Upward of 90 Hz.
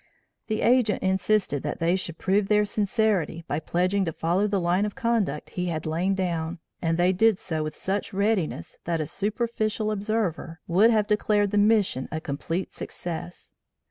Yes: high, 190 Hz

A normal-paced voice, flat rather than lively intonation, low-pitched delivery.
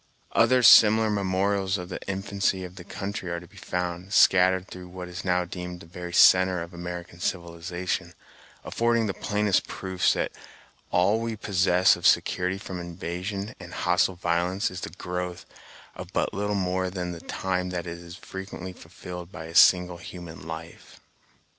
Yes: average, 165 wpm; narrow, 1.6 semitones; very low, 90 Hz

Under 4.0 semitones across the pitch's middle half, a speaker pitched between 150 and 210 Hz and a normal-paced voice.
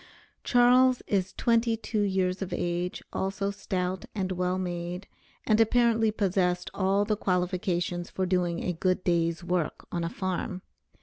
Yes: narrow, 2.5 semitones; medium, 185 Hz; average, 145 wpm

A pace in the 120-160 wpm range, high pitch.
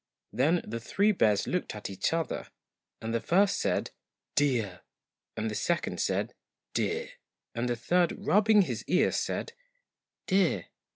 No: average, 155 wpm; medium, 160 Hz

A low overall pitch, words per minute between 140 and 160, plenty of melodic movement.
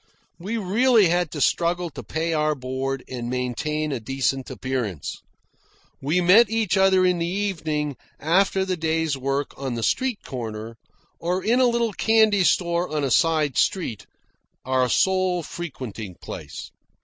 No: medium, 160 Hz; average, 150 wpm; wide, 5.9 semitones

